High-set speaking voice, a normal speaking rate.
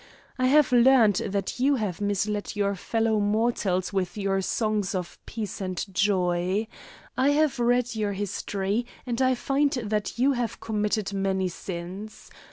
Yes: high, 210 Hz; average, 150 wpm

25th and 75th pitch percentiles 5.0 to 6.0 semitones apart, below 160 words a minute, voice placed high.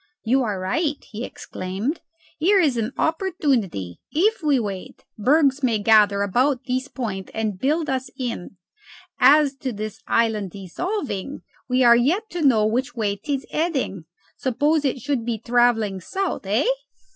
Yes: wide, 5.5 semitones; average, 150 wpm; very high, 250 Hz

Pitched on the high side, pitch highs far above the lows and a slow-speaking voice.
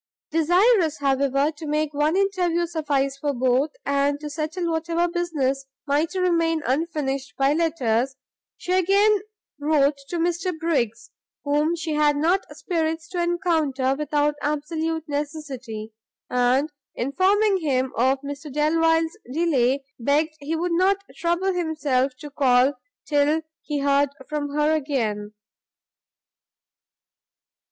No: very high, 300 Hz; average, 3.2 semitones; slow, 120 wpm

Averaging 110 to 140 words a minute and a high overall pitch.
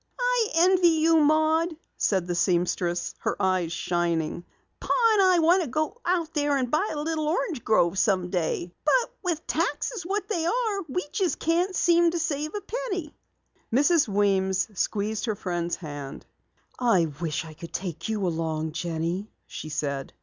No: average, 160 wpm; very high, 260 Hz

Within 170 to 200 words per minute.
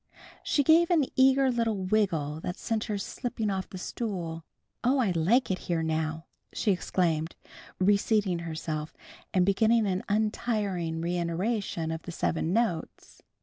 No: average, 145 wpm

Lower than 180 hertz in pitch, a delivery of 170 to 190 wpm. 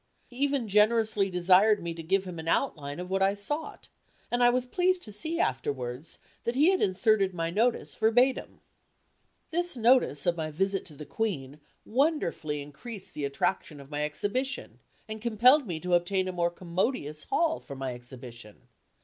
No: high, 195 Hz; average, 175 wpm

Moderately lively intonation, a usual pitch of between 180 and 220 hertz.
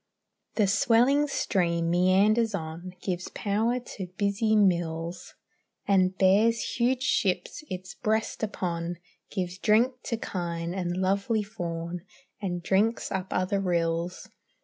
Yes: average, 3.6 semitones; high, 190 Hz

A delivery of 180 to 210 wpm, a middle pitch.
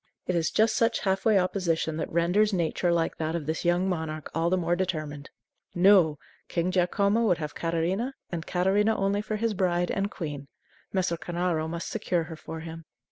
Yes: average, 190 wpm; medium, 175 Hz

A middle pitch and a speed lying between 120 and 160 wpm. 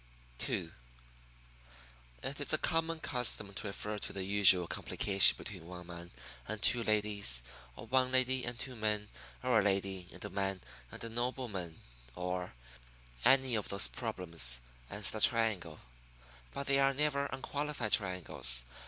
No: low, 105 Hz; average, 155 wpm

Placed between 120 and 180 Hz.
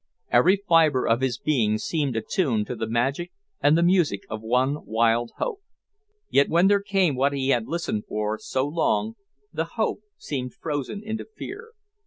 Yes: medium, 140 Hz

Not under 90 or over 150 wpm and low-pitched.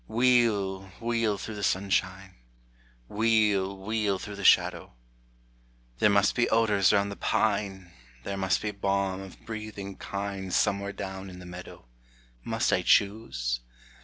Yes: slow, 135 wpm; low, 100 Hz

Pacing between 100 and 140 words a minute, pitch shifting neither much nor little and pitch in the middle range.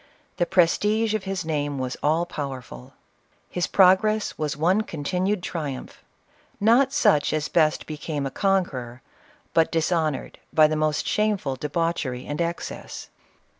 Yes: slow, 135 wpm; average, 4.5 semitones; medium, 165 Hz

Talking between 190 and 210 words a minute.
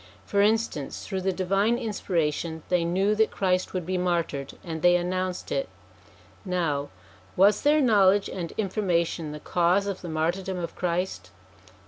No: average, 150 wpm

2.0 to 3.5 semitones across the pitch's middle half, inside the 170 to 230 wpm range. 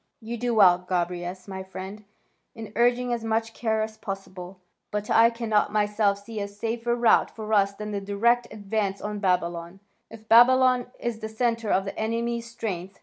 Yes: average, 2.8 semitones; average, 175 wpm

